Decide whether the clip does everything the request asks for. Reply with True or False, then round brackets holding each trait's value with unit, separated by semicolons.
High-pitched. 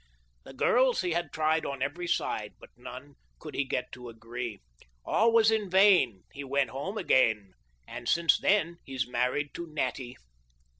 False (140 Hz)